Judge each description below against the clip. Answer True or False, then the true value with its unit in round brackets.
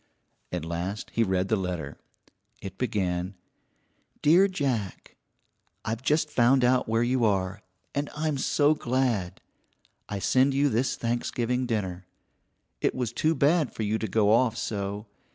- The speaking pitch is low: True (115 Hz)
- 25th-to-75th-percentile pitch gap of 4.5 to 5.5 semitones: True (4.9 semitones)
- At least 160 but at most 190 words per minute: False (145 wpm)